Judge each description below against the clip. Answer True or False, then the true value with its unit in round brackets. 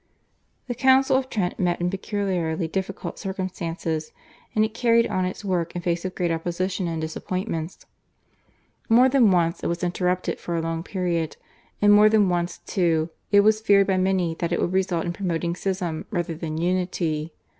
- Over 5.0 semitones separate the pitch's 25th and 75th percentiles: False (2.8 semitones)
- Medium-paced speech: True (175 wpm)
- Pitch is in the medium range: True (180 Hz)